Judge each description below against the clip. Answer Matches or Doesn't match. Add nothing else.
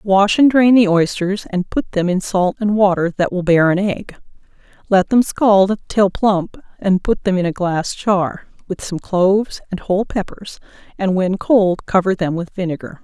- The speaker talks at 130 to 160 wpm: Doesn't match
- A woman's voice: Matches